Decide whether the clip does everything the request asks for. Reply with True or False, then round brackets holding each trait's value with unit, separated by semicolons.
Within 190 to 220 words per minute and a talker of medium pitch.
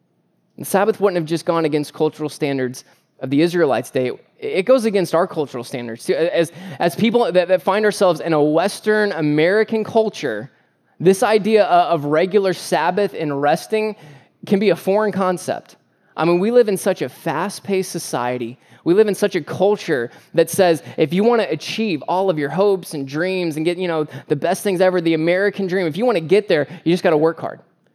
True (200 wpm; 175 Hz)